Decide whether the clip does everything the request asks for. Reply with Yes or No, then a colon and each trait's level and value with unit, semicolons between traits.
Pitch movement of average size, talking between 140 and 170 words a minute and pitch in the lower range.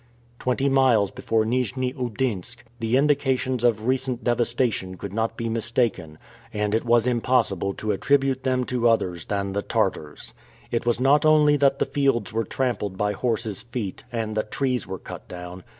Yes: average, 3.6 semitones; average, 165 wpm; low, 120 Hz